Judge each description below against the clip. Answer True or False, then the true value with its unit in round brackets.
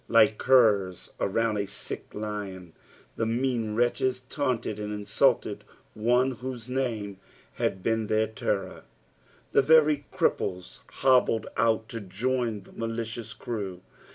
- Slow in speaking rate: True (125 wpm)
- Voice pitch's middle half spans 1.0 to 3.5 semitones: True (3.2 semitones)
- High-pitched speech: False (115 Hz)